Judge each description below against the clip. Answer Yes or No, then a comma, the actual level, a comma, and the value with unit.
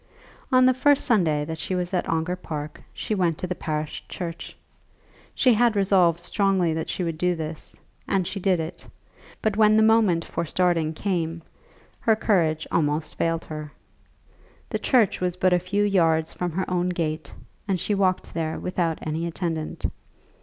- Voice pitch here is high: No, medium, 175 Hz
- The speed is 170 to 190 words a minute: Yes, average, 175 wpm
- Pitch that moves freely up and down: No, average, 3.3 semitones